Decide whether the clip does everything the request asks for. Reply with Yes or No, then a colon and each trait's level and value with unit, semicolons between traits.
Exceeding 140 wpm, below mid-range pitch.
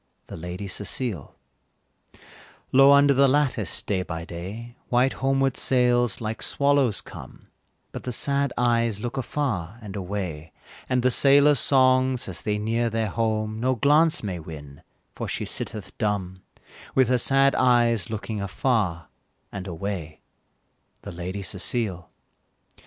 No: slow, 135 wpm; low, 115 Hz